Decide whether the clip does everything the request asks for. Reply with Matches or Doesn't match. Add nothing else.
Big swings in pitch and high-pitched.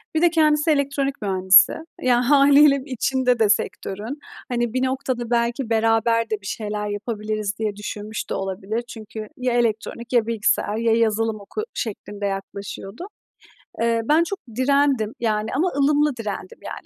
Doesn't match